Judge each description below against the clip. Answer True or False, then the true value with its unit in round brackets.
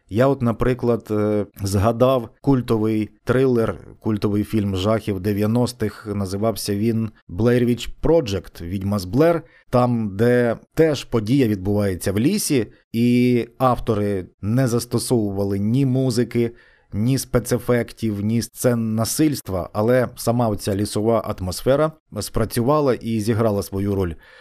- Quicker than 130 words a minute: False (110 wpm)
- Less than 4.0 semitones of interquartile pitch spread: True (3.0 semitones)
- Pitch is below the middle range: True (115 Hz)